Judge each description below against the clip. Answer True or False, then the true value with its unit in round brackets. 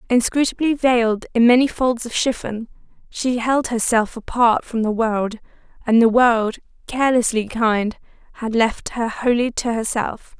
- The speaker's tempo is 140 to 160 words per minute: True (145 wpm)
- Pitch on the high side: True (235 Hz)